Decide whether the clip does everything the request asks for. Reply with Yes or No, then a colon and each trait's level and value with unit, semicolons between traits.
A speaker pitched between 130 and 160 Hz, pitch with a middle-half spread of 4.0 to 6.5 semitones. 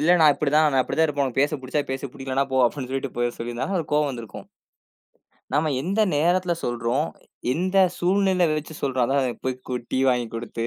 No: medium, 140 Hz; average, 3.6 semitones